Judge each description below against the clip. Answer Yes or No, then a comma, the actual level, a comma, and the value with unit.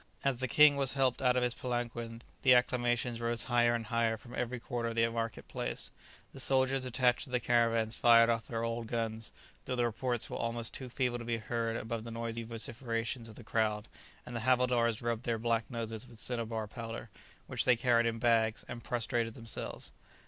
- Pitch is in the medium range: No, low, 115 Hz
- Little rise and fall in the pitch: Yes, narrow, 1.3 semitones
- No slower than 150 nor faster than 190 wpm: No, average, 200 wpm